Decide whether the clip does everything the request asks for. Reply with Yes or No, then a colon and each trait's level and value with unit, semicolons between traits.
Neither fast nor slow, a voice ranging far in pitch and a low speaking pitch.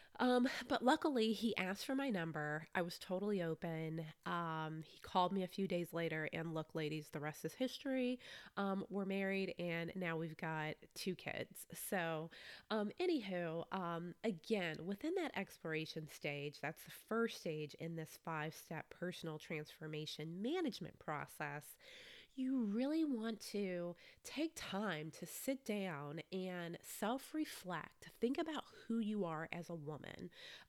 No: average, 150 wpm; wide, 6.1 semitones; medium, 180 Hz